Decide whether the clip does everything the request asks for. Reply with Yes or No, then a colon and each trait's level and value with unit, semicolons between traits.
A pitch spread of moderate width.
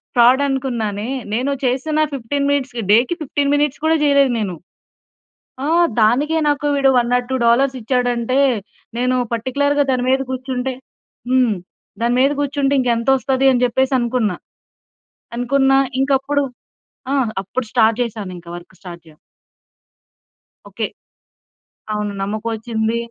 Yes: average, 3.1 semitones